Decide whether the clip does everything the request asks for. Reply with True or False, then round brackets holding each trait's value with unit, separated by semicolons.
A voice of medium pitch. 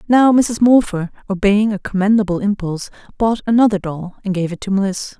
False (205 Hz)